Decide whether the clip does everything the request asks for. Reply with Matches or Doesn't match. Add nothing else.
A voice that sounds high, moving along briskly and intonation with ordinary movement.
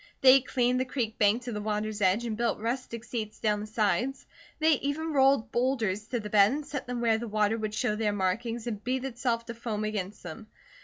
Matches